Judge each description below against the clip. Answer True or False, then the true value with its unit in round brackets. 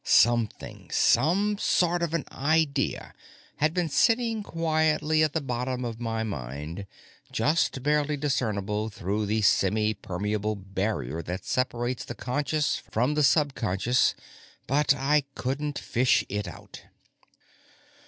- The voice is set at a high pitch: False (125 Hz)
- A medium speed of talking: False (120 wpm)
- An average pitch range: False (6.1 semitones)